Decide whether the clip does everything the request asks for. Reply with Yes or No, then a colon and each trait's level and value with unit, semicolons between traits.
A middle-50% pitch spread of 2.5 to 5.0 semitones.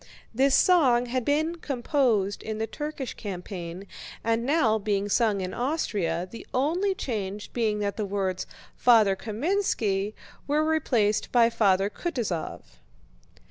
No: wide, 5.5 semitones